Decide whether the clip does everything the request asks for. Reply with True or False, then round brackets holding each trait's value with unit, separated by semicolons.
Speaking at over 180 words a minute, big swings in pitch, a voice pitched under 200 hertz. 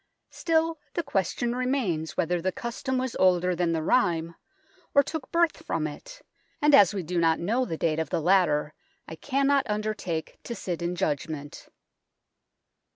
False (160 wpm; 7.9 semitones; 185 Hz)